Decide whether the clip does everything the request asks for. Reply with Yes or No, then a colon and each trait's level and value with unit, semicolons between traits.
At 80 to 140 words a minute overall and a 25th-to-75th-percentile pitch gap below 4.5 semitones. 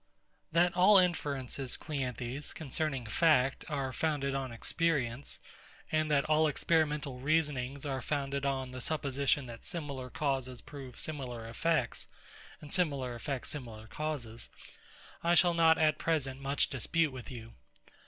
Yes: slow, 135 wpm; average, 3.4 semitones